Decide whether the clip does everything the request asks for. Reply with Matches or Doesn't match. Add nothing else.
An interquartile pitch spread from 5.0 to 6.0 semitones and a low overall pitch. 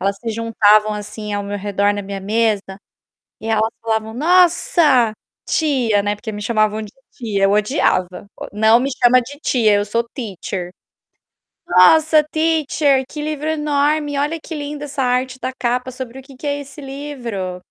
Doesn't match